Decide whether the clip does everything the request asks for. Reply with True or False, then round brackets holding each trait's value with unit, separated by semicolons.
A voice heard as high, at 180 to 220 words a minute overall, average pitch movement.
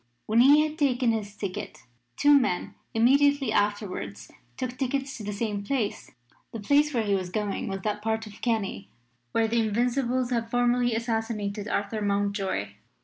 False (225 Hz; 160 wpm; 3.5 semitones)